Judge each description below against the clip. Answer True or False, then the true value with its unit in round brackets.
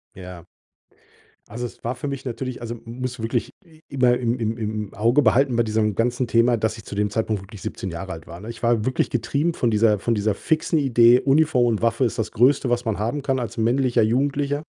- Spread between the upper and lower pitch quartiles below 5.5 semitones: True (2.9 semitones)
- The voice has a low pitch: True (120 Hz)